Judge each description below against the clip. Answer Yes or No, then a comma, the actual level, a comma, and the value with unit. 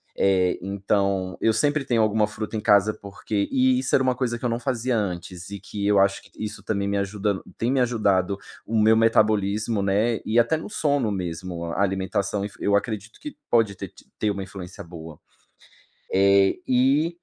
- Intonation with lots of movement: No, average, 3.0 semitones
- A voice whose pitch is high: No, low, 105 Hz